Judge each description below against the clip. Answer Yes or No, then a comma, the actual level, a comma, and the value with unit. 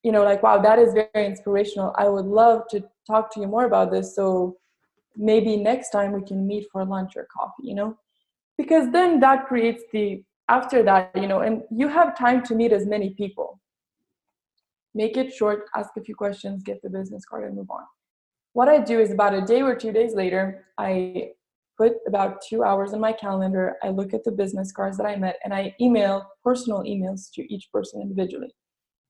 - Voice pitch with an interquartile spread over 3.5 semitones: No, average, 2.7 semitones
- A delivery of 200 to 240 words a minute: Yes, fast, 205 wpm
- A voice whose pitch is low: No, high, 210 Hz